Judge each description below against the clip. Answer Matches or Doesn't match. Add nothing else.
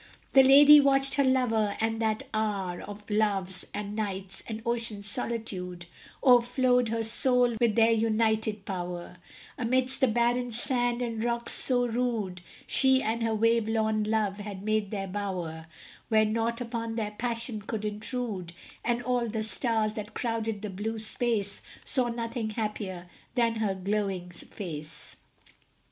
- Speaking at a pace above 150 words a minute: Doesn't match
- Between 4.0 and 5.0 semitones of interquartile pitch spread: Doesn't match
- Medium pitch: Doesn't match